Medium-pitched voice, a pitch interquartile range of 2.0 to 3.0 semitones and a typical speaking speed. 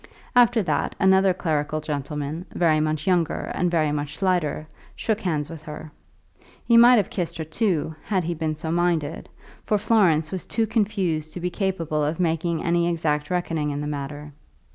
No: medium, 165 Hz; average, 3.5 semitones; average, 175 wpm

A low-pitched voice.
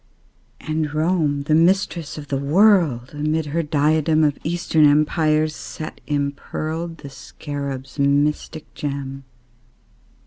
No: medium, 150 Hz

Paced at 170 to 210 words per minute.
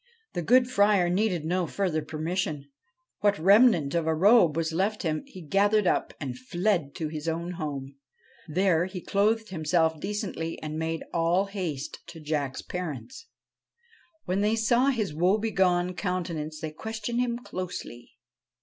No: average, 150 wpm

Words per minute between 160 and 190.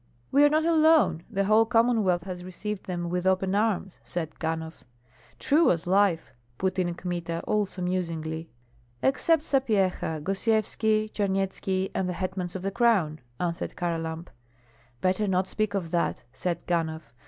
No: average, 145 wpm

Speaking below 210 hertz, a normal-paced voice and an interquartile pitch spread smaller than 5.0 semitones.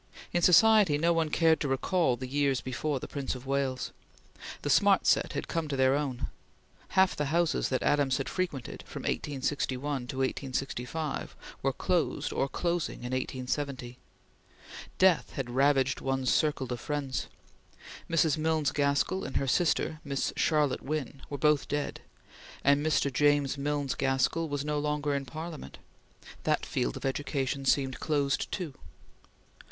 Yes: medium, 140 Hz; average, 150 wpm; narrow, 2.5 semitones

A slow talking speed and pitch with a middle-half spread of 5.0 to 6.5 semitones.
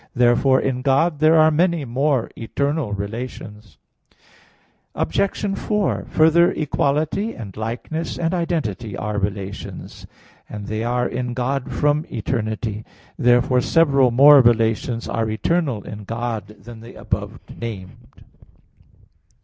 Yes: slow, 115 wpm; wide, 5.4 semitones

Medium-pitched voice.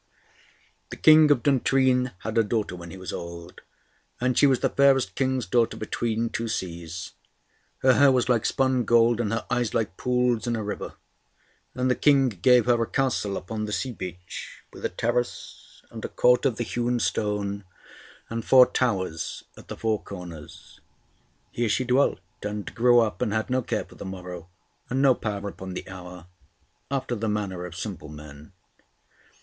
No: low, 115 Hz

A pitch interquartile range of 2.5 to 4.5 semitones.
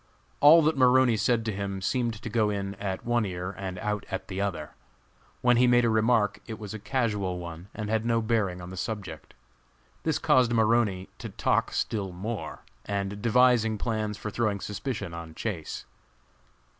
Yes: average, 3.3 semitones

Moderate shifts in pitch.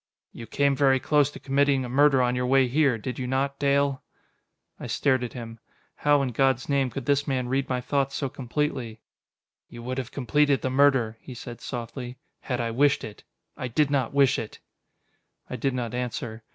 No: narrow, 2.2 semitones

